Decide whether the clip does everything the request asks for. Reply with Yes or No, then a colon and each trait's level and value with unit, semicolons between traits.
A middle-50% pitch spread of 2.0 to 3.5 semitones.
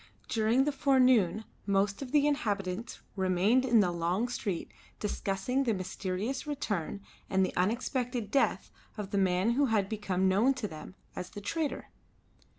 No: average, 5.0 semitones